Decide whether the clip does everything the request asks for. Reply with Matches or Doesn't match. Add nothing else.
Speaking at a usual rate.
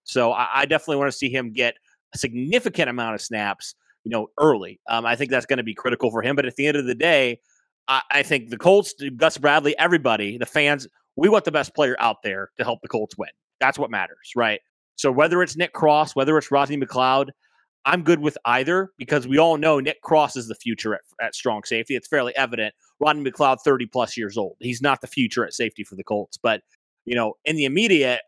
Doesn't match